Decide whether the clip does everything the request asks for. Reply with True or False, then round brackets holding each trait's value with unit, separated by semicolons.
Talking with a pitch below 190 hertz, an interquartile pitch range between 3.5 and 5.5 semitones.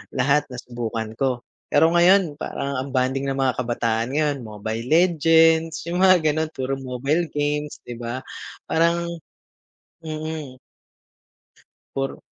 True (140 Hz; 4.1 semitones)